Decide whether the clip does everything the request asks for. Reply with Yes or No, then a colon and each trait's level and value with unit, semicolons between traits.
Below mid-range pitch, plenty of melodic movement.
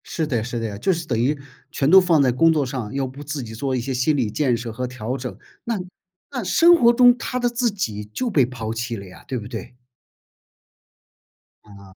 Yes: low, 130 Hz; wide, 6.1 semitones